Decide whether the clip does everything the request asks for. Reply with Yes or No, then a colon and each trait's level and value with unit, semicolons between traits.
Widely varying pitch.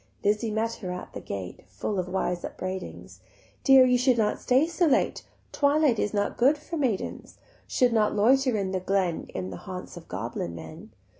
Yes: wide, 5.8 semitones